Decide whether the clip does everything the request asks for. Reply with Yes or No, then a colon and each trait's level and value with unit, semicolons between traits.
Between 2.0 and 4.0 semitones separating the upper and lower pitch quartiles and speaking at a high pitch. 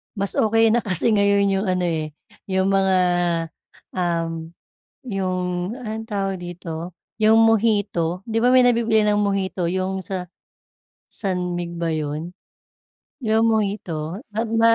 Yes: average, 3.5 semitones; high, 195 Hz